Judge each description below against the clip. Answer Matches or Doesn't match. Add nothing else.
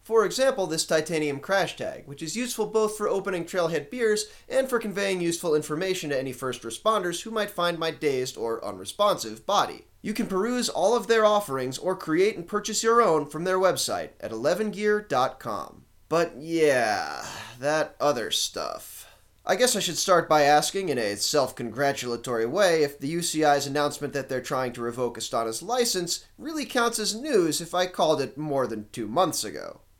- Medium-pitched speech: Matches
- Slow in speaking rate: Doesn't match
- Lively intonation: Matches